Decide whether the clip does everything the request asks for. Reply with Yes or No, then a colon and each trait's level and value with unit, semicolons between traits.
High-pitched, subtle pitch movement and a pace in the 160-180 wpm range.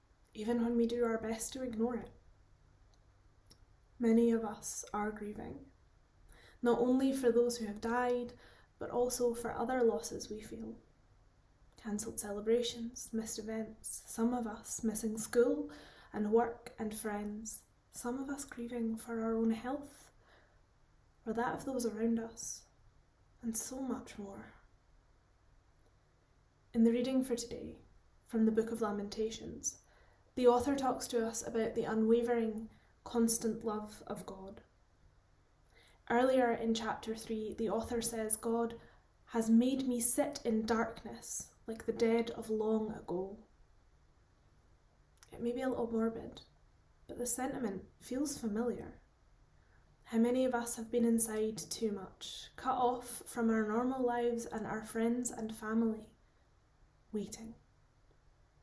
No: high, 225 Hz; narrow, 2.3 semitones; slow, 135 wpm